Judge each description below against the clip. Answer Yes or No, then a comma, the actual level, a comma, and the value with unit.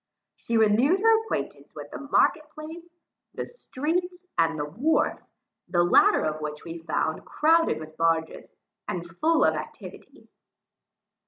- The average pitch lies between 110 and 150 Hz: No, high, 240 Hz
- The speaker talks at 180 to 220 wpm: No, average, 140 wpm